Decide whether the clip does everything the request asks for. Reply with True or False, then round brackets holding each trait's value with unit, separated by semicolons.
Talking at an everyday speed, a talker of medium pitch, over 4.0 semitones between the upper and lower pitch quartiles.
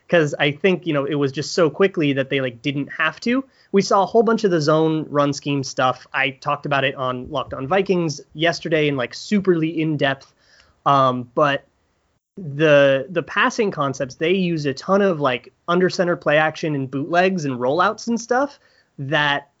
True (195 wpm; 150 Hz; 4.7 semitones)